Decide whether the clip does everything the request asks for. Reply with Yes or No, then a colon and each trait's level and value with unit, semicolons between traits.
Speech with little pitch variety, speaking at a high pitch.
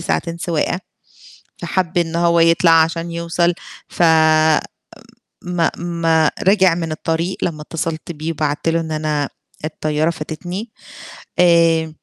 No: narrow, 1.3 semitones; medium, 165 Hz